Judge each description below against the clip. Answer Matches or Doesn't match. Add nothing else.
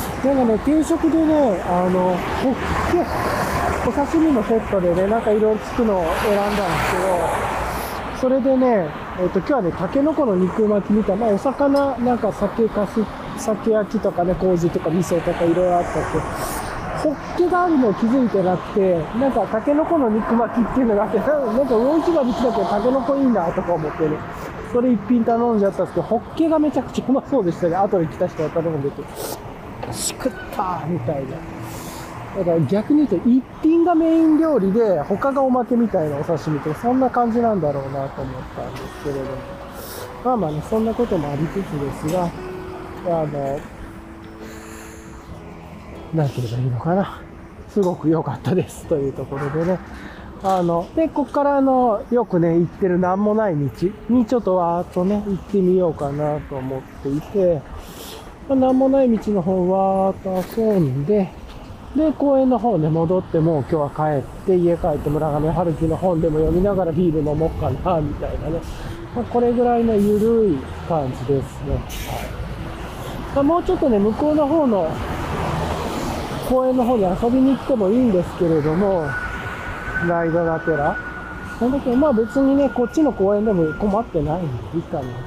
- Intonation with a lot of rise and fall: Matches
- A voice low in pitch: Doesn't match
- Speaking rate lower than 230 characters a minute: Doesn't match